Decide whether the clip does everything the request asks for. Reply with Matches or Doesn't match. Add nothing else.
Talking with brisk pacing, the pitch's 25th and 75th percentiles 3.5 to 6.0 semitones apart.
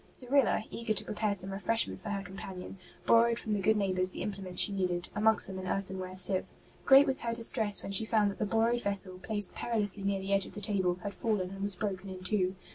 Doesn't match